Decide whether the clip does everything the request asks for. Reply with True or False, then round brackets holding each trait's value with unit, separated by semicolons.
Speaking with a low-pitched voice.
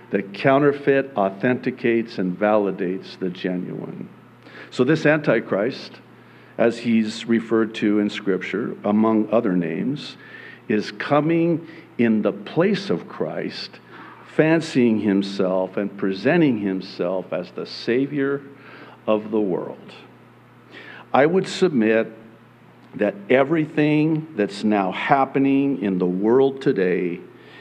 True (115 Hz)